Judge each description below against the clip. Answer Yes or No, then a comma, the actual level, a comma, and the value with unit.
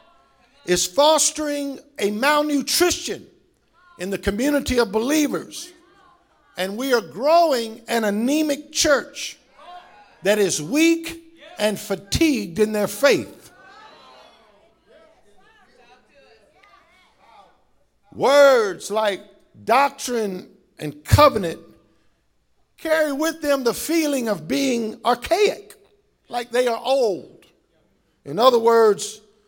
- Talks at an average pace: No, slow, 90 wpm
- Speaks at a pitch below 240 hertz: No, very high, 270 Hz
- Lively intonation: Yes, wide, 6.6 semitones